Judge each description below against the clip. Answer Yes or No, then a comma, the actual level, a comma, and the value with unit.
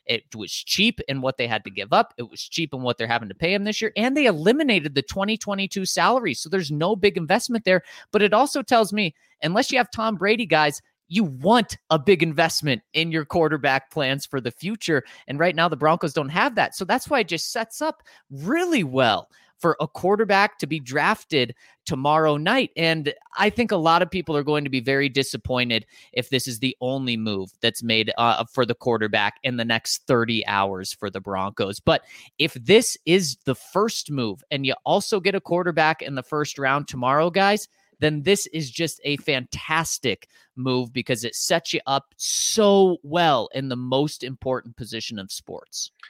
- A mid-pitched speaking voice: Yes, medium, 155 Hz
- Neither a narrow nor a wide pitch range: No, wide, 7.3 semitones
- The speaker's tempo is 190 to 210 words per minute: Yes, average, 200 wpm